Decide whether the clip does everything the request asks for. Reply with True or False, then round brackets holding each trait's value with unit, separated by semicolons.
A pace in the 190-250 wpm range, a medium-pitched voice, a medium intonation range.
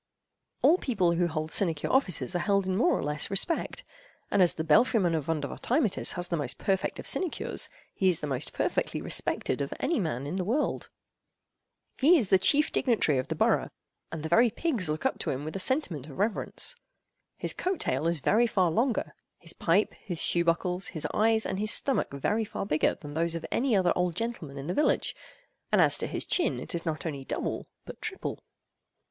False (200 wpm; 180 Hz; 6.0 semitones)